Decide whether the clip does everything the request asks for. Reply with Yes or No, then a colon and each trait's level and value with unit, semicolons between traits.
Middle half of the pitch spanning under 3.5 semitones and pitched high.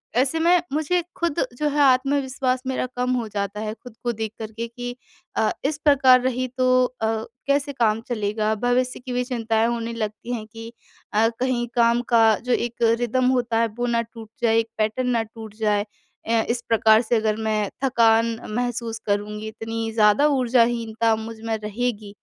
Yes: narrow, 2.4 semitones; high, 235 Hz